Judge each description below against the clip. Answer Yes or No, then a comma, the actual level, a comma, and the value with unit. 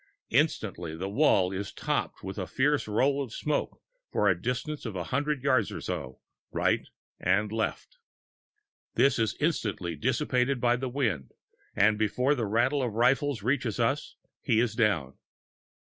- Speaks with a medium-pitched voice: No, low, 115 Hz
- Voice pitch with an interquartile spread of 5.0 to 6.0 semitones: Yes, wide, 5.4 semitones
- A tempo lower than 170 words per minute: Yes, average, 160 wpm